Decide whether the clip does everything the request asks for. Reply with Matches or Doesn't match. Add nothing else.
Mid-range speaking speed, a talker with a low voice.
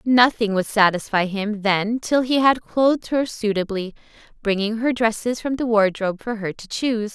Doesn't match